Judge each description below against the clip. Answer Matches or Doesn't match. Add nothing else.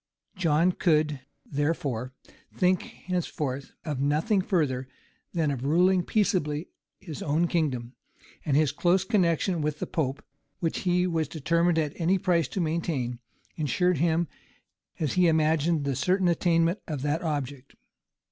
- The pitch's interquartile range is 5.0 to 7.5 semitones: Doesn't match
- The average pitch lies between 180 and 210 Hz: Doesn't match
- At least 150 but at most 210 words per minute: Doesn't match